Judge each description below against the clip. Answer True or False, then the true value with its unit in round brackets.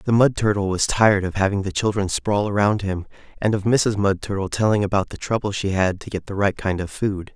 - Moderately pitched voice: False (100 Hz)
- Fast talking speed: True (245 wpm)